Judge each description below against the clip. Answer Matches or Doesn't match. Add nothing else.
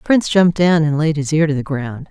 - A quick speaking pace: Matches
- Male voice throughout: Doesn't match